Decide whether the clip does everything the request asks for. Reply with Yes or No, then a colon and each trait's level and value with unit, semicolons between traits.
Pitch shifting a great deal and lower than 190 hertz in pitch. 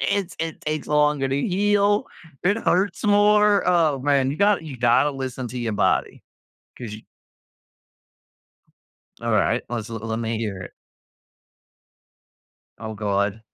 Yes: wide, 8.8 semitones; medium, 140 Hz